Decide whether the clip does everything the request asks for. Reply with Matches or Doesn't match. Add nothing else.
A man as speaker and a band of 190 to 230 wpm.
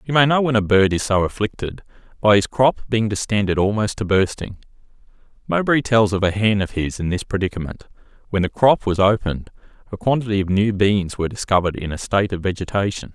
Matches